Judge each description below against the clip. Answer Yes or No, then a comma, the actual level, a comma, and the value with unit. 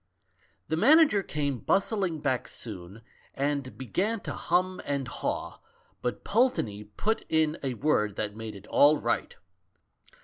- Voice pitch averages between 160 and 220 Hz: No, medium, 145 Hz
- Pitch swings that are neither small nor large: No, wide, 8.4 semitones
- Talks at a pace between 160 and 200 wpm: No, slow, 135 wpm